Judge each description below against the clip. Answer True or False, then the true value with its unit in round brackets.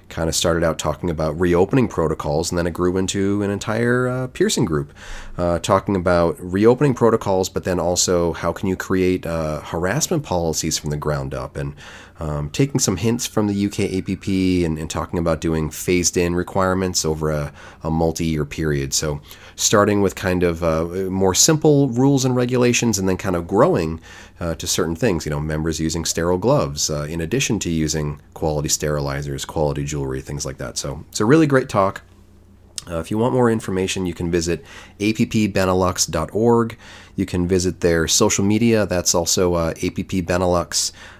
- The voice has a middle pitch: False (90 Hz)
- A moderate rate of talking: True (180 wpm)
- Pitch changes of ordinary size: True (3.8 semitones)